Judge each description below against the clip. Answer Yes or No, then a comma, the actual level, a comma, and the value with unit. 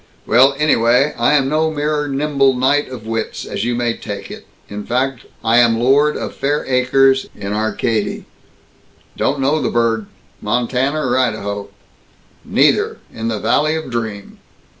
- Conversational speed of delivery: Yes, average, 155 wpm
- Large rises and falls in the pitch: No, average, 3.8 semitones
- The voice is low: Yes, low, 125 Hz